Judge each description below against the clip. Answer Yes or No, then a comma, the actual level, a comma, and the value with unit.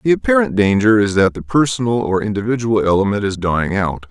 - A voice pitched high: No, low, 105 Hz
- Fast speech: No, average, 190 wpm